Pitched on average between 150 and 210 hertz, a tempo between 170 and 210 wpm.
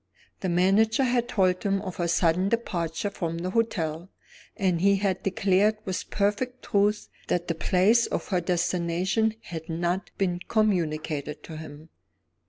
No: medium, 185 Hz; average, 145 wpm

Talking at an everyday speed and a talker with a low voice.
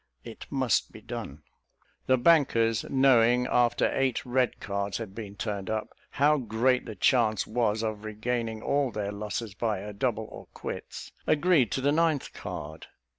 Yes: average, 160 wpm; low, 115 Hz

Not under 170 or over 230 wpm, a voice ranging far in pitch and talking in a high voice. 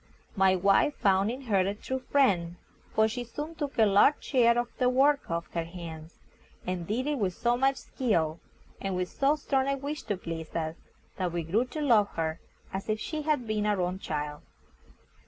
Yes: average, 200 wpm; wide, 6.8 semitones; high, 210 Hz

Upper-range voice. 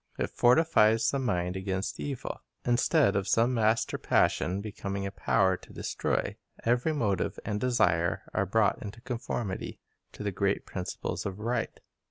No: low, 105 Hz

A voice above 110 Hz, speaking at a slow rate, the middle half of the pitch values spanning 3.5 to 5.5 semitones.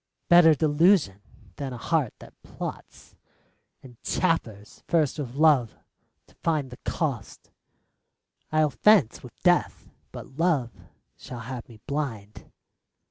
Yes: medium, 140 Hz; slow, 120 wpm; average, 5.1 semitones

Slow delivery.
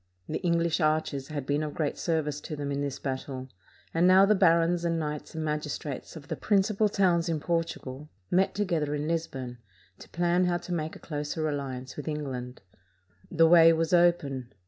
No: average, 190 wpm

